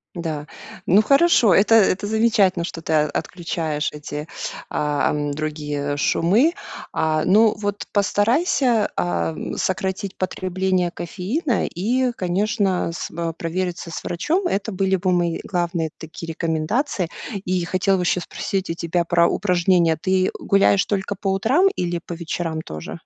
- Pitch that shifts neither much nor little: Yes, average, 3.6 semitones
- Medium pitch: Yes, medium, 180 Hz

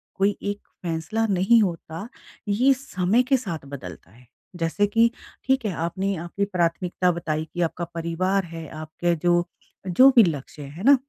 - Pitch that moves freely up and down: No, average, 3.9 semitones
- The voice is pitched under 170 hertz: No, medium, 180 Hz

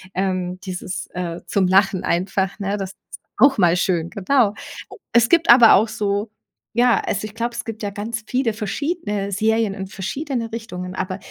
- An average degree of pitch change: Yes, average, 3.5 semitones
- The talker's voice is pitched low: No, high, 205 Hz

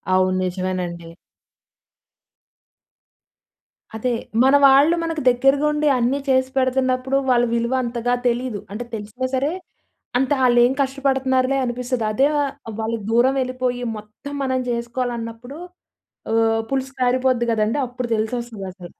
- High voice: Yes, high, 245 Hz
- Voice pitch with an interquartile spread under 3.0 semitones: Yes, narrow, 2.5 semitones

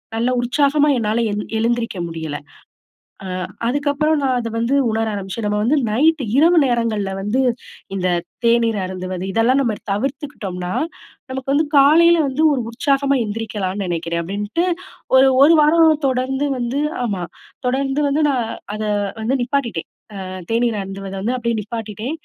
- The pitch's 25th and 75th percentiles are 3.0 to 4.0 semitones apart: No, average, 5.0 semitones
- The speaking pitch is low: No, high, 235 Hz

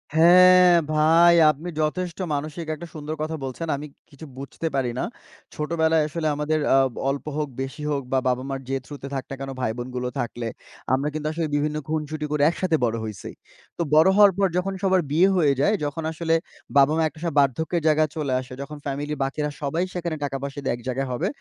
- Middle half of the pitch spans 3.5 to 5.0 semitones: No, average, 3.0 semitones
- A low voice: No, medium, 150 Hz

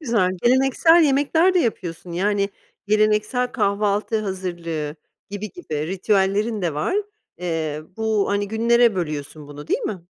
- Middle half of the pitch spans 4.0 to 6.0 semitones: Yes, average, 5.1 semitones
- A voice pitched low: No, high, 205 Hz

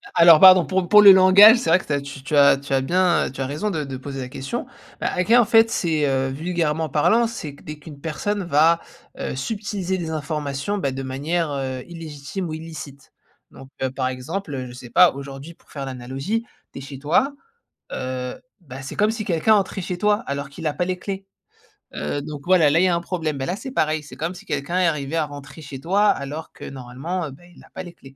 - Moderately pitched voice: Yes, medium, 155 Hz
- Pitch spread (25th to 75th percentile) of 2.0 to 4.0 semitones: No, average, 4.9 semitones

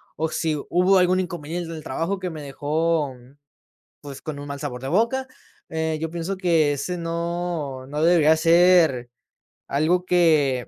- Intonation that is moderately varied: Yes, average, 3.3 semitones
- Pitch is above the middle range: No, medium, 160 Hz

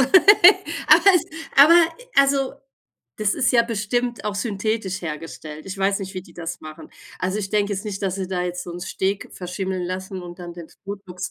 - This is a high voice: Yes, high, 195 Hz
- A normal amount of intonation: Yes, average, 3.1 semitones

